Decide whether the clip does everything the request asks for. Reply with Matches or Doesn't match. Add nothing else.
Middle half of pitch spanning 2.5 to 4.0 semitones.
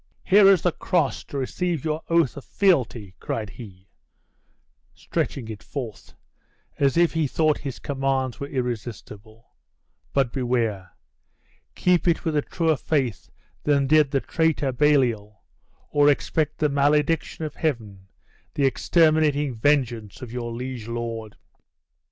Doesn't match